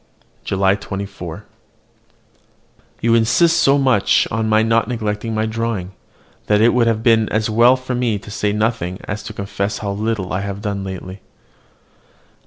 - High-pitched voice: No, low, 110 Hz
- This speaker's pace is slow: No, average, 155 wpm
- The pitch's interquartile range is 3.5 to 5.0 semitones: No, narrow, 2.4 semitones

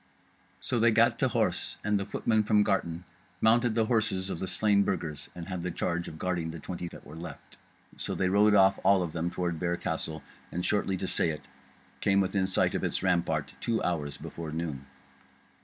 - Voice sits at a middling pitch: No, very low, 90 Hz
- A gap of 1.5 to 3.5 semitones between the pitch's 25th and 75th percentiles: Yes, average, 3.2 semitones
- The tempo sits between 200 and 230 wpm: Yes, fast, 205 wpm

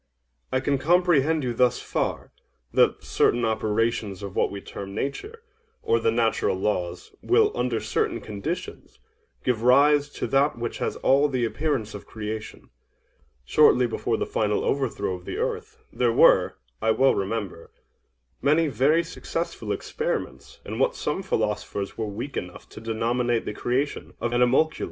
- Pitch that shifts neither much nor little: Yes, average, 5.0 semitones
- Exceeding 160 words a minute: No, average, 150 wpm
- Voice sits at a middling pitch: No, low, 120 Hz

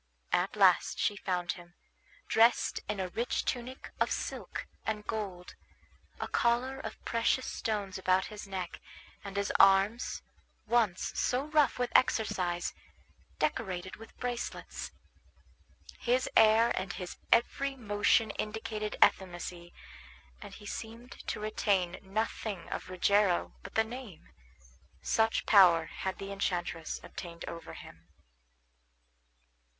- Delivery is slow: Yes, slow, 120 wpm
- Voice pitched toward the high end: Yes, high, 205 Hz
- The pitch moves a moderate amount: Yes, average, 3.7 semitones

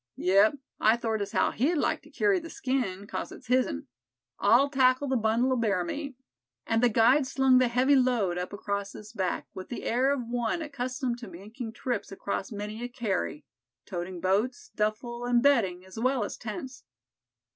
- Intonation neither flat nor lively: Yes, average, 4.1 semitones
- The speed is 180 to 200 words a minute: Yes, average, 185 wpm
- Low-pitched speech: No, high, 235 Hz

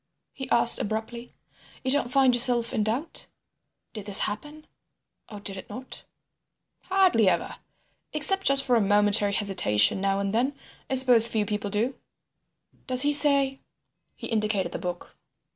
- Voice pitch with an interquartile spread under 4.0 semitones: No, average, 4.5 semitones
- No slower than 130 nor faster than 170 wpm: Yes, average, 150 wpm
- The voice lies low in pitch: No, high, 235 Hz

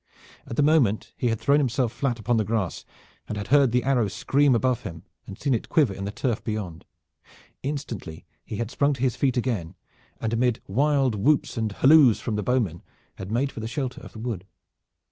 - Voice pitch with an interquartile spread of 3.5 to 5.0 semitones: Yes, average, 4.1 semitones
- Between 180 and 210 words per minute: Yes, fast, 205 wpm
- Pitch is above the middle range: No, low, 120 Hz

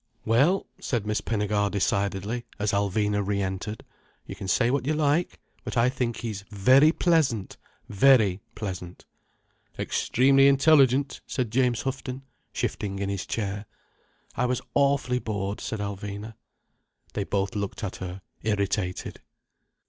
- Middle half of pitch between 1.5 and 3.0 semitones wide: No, average, 4.4 semitones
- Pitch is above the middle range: No, low, 110 Hz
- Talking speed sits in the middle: No, slow, 130 wpm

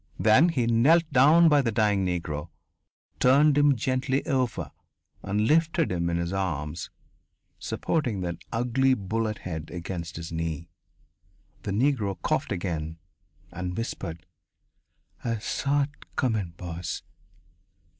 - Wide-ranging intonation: Yes, wide, 7.5 semitones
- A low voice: Yes, low, 105 Hz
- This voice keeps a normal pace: No, slow, 125 wpm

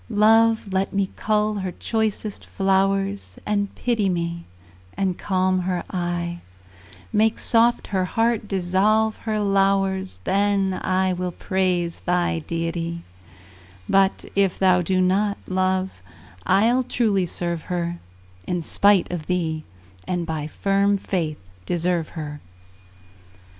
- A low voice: No, high, 190 Hz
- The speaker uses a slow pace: Yes, slow, 120 wpm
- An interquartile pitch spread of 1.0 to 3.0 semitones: Yes, narrow, 2.5 semitones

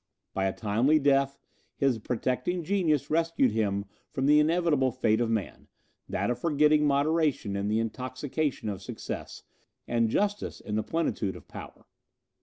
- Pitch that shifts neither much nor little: No, wide, 5.7 semitones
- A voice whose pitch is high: No, low, 135 Hz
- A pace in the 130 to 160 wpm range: Yes, average, 150 wpm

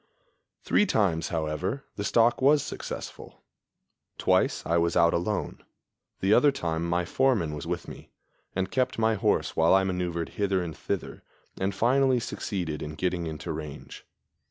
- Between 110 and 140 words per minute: No, average, 155 wpm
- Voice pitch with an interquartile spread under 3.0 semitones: No, average, 5.2 semitones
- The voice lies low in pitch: Yes, very low, 90 Hz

